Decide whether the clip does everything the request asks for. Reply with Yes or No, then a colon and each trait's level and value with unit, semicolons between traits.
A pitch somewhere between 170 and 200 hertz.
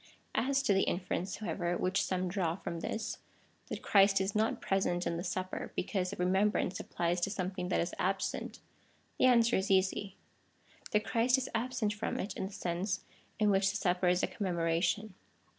Yes: high, 190 Hz